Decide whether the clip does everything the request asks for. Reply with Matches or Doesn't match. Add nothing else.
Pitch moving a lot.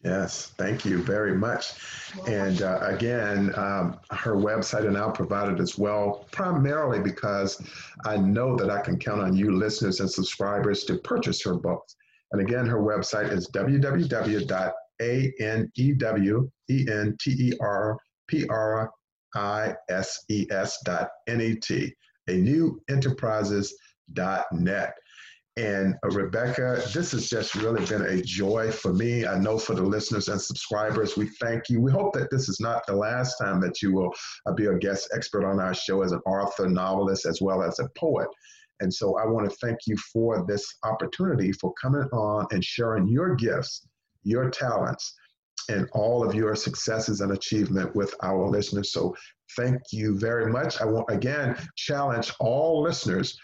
Doesn't match